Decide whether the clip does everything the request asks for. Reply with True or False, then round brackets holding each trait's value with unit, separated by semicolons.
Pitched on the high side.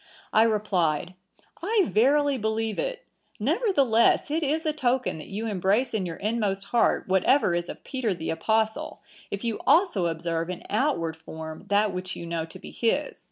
True (215 Hz)